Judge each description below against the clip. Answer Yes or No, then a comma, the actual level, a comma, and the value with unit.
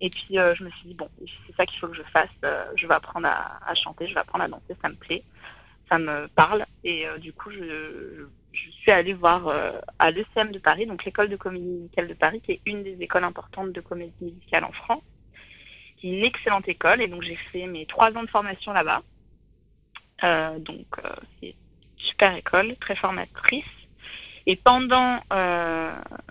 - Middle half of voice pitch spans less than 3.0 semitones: No, average, 3.4 semitones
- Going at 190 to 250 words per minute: Yes, average, 210 wpm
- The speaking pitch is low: No, medium, 185 Hz